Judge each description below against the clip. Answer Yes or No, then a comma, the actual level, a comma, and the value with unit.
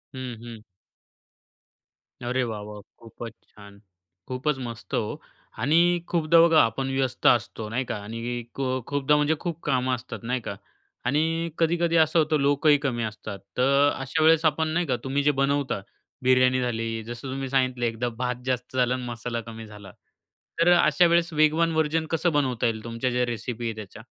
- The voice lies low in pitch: Yes, low, 130 Hz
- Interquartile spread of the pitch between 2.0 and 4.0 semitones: No, average, 4.4 semitones